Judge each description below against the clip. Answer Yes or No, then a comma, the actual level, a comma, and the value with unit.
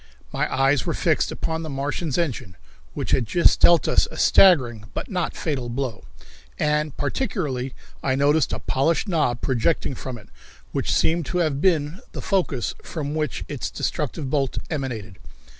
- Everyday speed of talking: Yes, average, 160 wpm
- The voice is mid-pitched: Yes, medium, 145 Hz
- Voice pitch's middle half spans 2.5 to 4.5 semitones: Yes, average, 3.9 semitones